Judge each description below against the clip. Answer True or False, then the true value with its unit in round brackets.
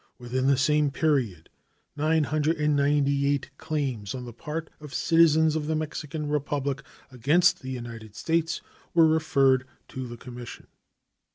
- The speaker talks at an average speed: False (125 wpm)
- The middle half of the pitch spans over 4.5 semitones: False (3.0 semitones)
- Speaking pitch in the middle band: True (145 Hz)